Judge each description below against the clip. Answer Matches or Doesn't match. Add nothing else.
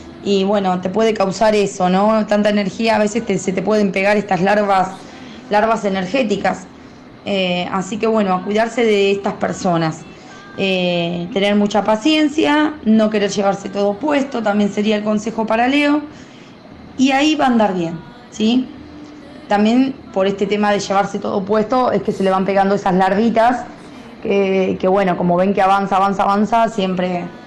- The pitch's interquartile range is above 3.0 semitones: Doesn't match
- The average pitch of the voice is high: Matches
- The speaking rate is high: Doesn't match